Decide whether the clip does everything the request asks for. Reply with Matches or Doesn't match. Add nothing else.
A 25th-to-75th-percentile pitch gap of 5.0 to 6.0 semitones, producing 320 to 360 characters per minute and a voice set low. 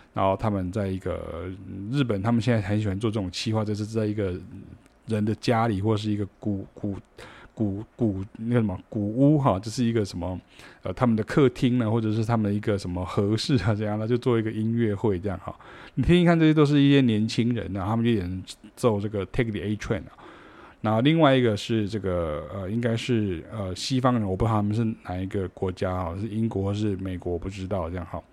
Doesn't match